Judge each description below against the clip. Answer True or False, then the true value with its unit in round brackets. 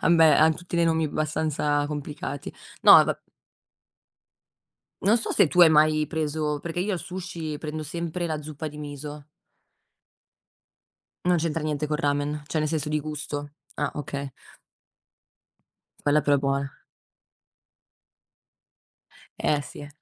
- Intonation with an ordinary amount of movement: False (1.7 semitones)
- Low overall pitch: False (150 Hz)